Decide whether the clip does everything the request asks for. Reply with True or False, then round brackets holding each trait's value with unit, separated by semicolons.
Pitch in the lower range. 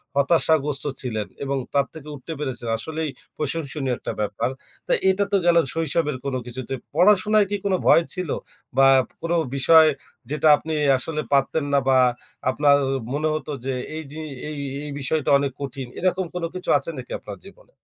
False (150 Hz)